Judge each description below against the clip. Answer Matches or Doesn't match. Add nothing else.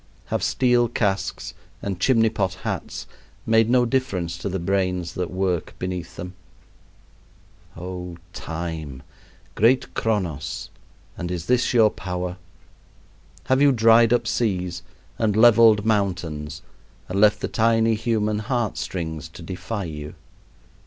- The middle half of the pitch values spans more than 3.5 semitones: Matches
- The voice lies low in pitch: Matches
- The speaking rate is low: Matches